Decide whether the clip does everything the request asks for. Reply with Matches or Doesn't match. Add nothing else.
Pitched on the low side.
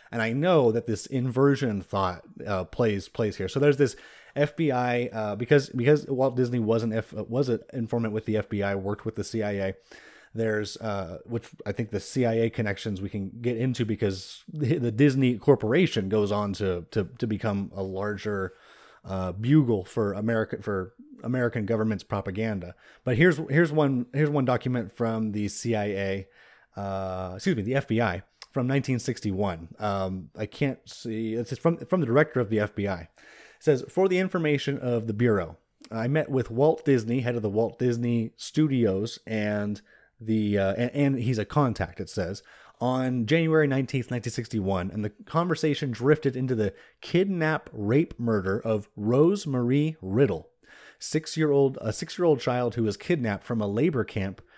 Matches